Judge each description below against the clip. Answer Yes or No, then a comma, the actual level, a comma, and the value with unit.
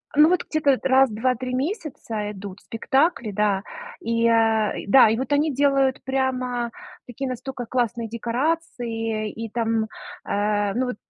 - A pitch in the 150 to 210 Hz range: No, high, 240 Hz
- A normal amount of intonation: Yes, average, 3.2 semitones